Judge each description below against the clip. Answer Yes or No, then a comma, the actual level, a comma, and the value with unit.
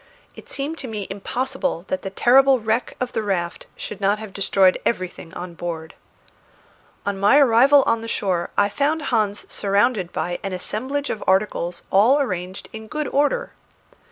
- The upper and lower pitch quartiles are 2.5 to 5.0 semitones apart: No, wide, 5.6 semitones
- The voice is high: Yes, high, 210 Hz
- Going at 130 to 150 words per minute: No, average, 165 wpm